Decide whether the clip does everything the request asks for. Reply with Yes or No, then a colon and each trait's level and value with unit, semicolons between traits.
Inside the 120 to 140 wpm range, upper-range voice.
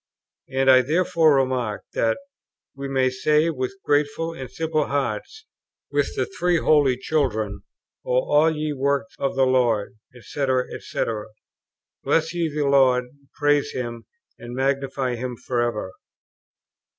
No: slow, 135 wpm; low, 135 Hz